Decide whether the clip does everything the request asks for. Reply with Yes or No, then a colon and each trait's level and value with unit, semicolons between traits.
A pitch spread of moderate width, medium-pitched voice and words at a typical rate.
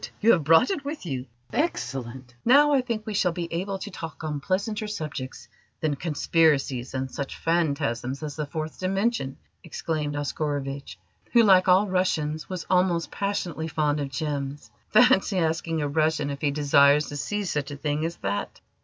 Yes: average, 4.7 semitones; medium, 155 Hz; average, 170 wpm